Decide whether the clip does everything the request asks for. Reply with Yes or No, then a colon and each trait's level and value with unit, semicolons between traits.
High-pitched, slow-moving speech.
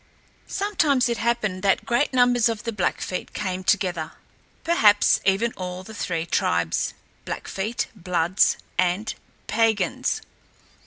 Yes: high, 205 Hz; slow, 120 wpm